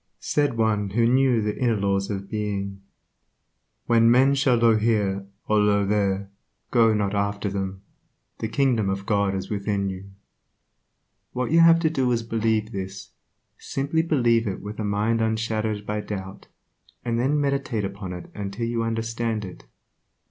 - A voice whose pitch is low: Yes, low, 110 Hz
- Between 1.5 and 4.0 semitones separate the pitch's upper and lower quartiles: Yes, average, 2.8 semitones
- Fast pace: No, average, 165 wpm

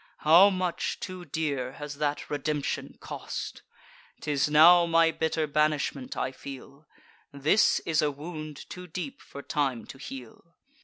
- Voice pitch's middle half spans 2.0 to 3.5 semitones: Yes, average, 2.8 semitones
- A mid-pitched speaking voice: Yes, medium, 150 Hz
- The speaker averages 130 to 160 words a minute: Yes, average, 140 wpm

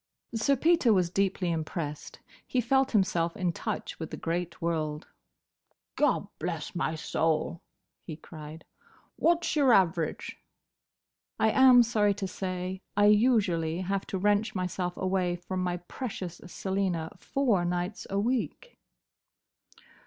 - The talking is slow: Yes, slow, 125 wpm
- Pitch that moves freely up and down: No, average, 4.2 semitones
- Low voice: No, medium, 185 Hz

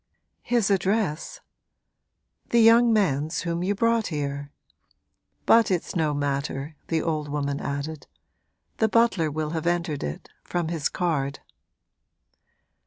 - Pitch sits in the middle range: Yes, medium, 160 Hz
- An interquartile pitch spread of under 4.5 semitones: No, wide, 5.4 semitones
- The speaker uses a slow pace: Yes, slow, 120 wpm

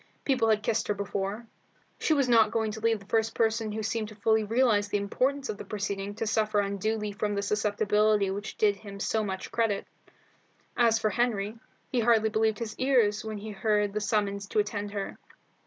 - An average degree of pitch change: No, narrow, 1.6 semitones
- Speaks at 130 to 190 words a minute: No, fast, 205 wpm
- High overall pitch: Yes, high, 215 Hz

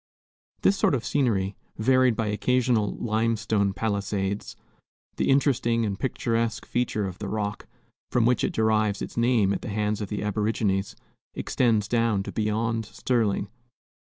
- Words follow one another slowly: No, average, 145 wpm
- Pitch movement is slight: Yes, narrow, 2.3 semitones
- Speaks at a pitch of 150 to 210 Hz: No, low, 110 Hz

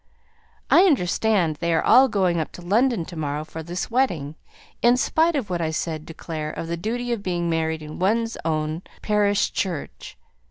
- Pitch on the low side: No, medium, 175 Hz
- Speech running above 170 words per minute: Yes, average, 190 wpm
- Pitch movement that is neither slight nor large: No, wide, 5.7 semitones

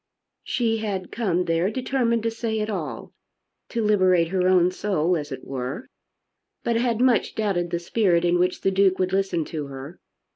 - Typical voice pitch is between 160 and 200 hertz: Yes, medium, 185 Hz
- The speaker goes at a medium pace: Yes, average, 180 wpm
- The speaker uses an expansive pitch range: No, average, 4.3 semitones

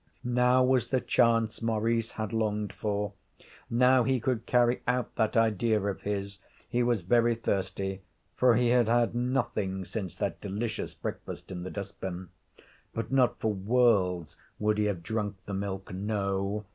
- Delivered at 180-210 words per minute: No, average, 160 wpm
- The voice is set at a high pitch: No, low, 110 Hz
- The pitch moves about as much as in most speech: Yes, average, 3.4 semitones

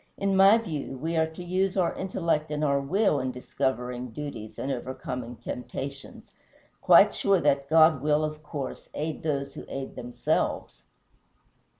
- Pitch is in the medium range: Yes, medium, 145 Hz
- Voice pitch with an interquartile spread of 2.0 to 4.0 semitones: Yes, average, 3.7 semitones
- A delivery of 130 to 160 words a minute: Yes, average, 155 wpm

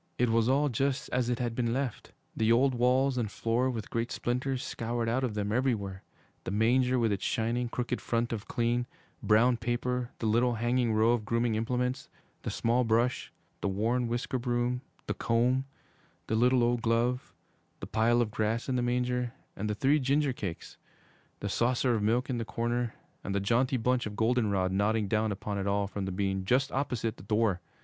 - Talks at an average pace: Yes, average, 195 wpm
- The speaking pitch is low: Yes, low, 120 Hz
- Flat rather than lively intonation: Yes, narrow, 2.2 semitones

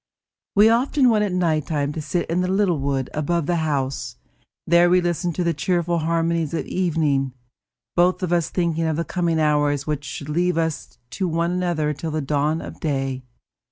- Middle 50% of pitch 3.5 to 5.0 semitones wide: No, average, 2.8 semitones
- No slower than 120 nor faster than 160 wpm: No, average, 190 wpm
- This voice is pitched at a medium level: Yes, medium, 165 Hz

